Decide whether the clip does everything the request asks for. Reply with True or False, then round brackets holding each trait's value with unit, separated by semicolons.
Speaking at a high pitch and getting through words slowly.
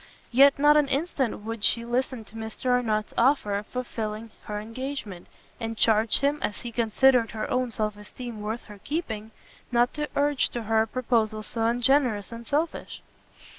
False (230 Hz; 170 wpm)